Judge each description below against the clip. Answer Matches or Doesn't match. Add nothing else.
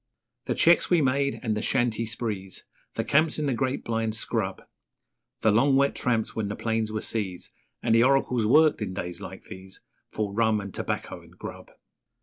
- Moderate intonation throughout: Matches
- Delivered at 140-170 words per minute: Doesn't match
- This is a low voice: Matches